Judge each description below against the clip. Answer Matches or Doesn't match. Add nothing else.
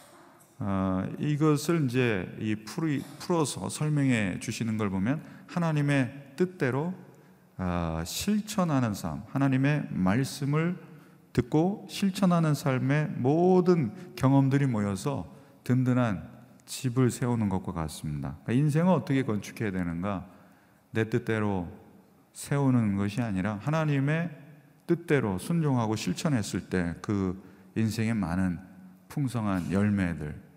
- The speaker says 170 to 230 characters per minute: Doesn't match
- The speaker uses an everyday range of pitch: Doesn't match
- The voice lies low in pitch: Matches